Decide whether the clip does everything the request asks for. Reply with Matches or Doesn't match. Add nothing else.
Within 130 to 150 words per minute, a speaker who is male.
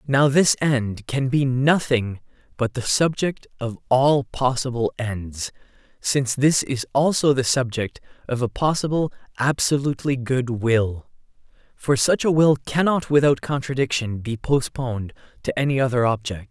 Matches